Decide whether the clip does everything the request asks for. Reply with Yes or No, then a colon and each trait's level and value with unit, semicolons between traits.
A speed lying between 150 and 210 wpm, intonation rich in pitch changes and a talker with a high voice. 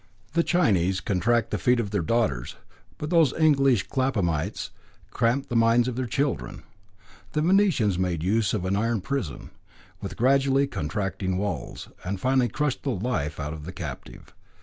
No: average, 160 wpm; wide, 6.4 semitones; low, 115 Hz